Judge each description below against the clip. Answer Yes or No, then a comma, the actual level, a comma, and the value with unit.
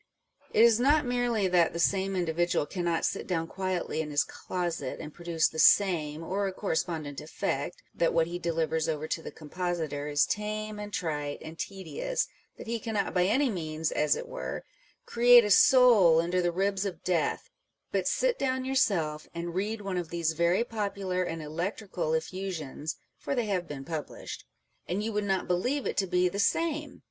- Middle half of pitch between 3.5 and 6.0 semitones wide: Yes, average, 4.3 semitones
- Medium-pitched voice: Yes, medium, 180 Hz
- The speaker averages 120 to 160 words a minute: No, average, 195 wpm